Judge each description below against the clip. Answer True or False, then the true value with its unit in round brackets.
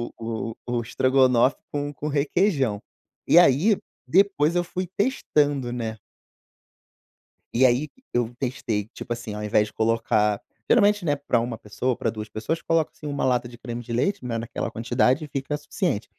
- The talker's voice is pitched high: False (125 Hz)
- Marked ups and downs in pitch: False (4.6 semitones)